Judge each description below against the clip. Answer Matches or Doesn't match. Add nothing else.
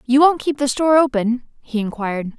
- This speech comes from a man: Doesn't match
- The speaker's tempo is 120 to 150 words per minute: Doesn't match